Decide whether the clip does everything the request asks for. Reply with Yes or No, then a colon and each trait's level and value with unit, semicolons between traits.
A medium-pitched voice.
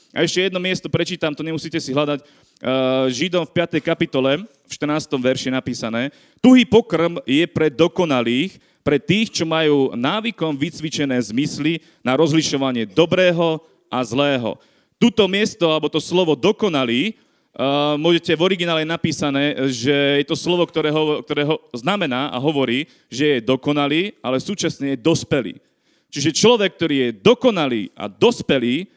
Yes: medium, 155 Hz